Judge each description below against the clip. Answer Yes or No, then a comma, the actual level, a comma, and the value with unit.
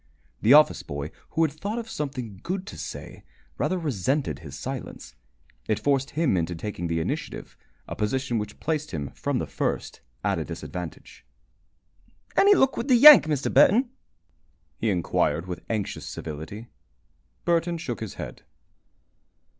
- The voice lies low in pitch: Yes, low, 130 Hz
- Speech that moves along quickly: No, average, 150 wpm